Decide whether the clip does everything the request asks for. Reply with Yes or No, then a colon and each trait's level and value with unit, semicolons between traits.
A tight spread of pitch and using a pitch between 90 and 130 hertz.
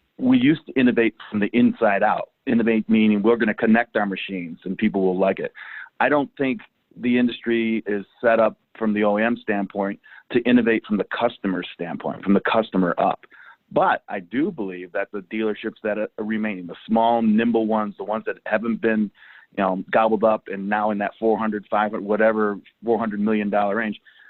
Yes: narrow, 1.9 semitones; low, 110 Hz